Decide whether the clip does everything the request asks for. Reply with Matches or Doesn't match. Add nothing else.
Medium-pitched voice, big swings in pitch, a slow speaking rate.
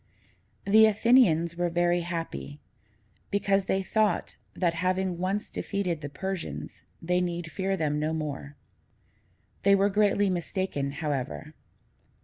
Doesn't match